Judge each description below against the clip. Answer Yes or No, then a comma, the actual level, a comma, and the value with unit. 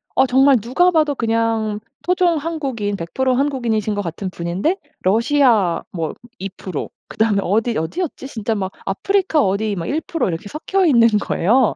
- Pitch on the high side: Yes, high, 230 Hz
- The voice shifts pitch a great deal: Yes, wide, 6.5 semitones